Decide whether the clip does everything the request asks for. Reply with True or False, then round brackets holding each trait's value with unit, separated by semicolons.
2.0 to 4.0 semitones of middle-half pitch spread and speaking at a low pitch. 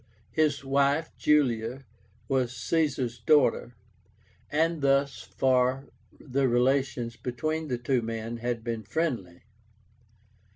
True (3.0 semitones; 130 Hz)